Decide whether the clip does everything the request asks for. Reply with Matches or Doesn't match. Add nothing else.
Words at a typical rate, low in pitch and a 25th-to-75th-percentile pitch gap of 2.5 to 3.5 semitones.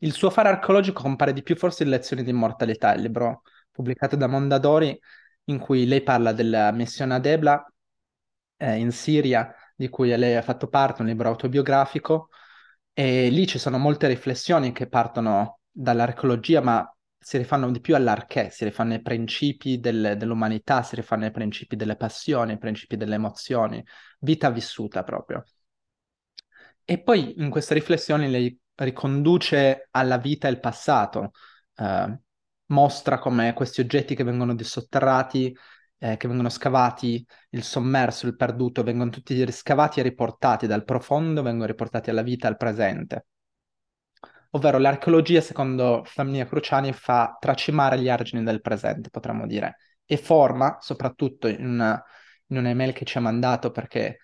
Matches